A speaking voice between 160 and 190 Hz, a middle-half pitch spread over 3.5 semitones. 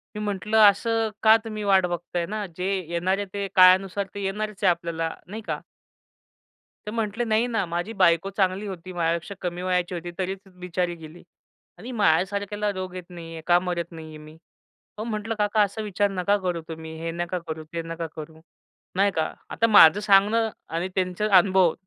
No: medium, 185 Hz; average, 3.1 semitones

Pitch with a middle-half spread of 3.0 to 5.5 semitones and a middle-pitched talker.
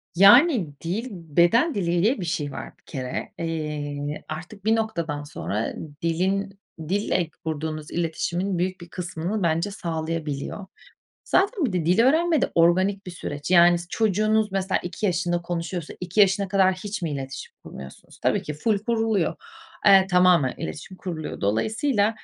Yes: average, 4.0 semitones; medium, 180 Hz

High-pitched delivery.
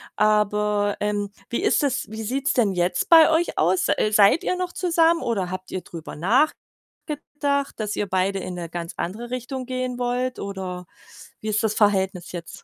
Yes: high, 210 Hz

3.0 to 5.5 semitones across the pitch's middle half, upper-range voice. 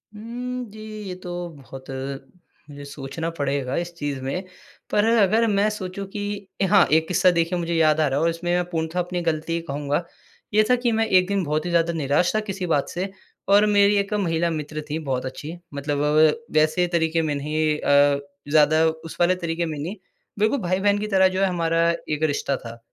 No: average, 4.1 semitones; medium, 170 Hz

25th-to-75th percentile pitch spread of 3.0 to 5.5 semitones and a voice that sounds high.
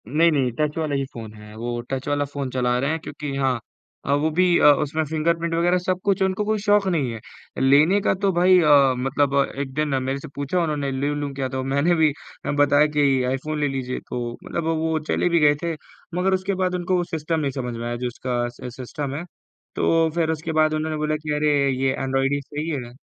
No: average, 3.5 semitones; medium, 150 Hz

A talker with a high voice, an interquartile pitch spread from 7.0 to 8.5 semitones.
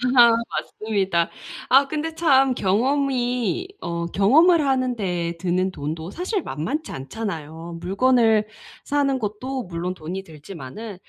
Yes: high, 215 Hz; wide, 7.5 semitones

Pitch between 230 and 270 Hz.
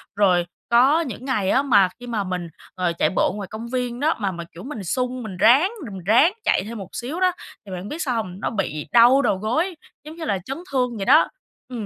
Yes: high, 235 Hz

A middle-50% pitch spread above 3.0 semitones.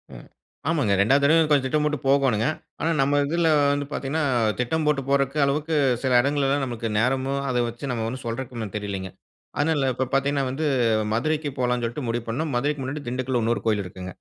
Yes: average, 3.5 semitones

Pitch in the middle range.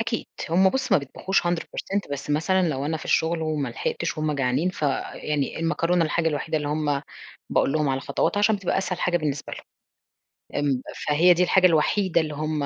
Yes: medium, 160 Hz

